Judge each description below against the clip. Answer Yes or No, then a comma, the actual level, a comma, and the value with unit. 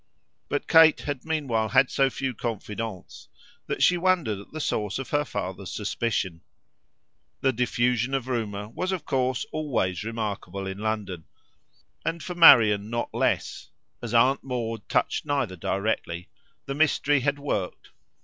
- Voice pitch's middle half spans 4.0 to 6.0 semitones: Yes, average, 5.3 semitones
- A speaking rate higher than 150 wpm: No, average, 145 wpm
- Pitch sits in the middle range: No, low, 120 Hz